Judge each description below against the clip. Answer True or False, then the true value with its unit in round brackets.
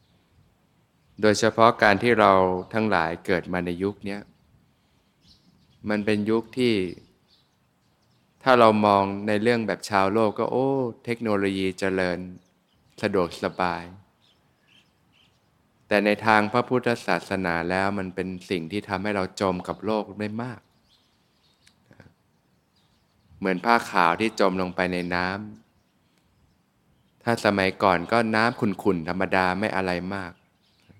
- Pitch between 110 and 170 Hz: False (100 Hz)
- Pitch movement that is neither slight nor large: True (3.0 semitones)